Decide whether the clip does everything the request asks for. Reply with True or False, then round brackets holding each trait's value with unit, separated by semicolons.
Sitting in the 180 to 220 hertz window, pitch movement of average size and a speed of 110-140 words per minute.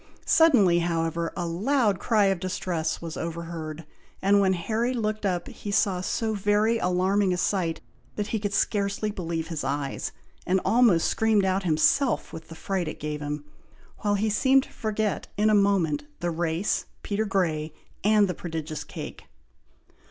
False (190 Hz; 4.1 semitones; 170 wpm)